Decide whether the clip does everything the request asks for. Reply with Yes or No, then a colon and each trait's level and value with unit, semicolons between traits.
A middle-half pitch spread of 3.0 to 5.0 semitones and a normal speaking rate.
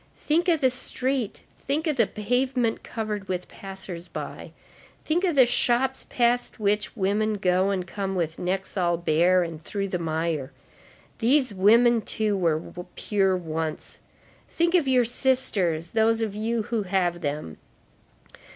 No: wide, 5.4 semitones; average, 150 wpm